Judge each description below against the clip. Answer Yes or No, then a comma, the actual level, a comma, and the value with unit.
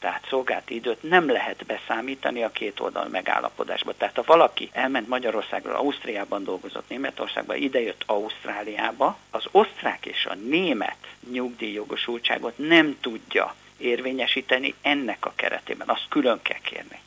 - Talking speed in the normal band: Yes, average, 125 wpm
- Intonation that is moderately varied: No, narrow, 2.1 semitones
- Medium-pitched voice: No, low, 125 Hz